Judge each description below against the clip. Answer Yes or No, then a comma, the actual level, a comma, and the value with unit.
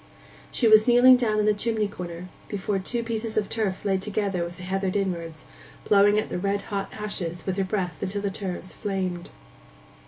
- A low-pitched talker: No, high, 200 Hz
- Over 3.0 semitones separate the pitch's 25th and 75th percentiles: No, narrow, 2.5 semitones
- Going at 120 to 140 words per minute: No, average, 190 wpm